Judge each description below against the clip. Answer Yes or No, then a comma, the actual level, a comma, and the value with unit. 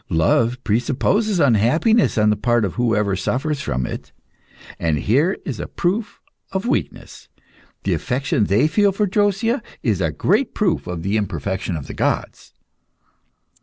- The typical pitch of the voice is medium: No, low, 125 Hz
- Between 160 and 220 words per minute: No, average, 145 wpm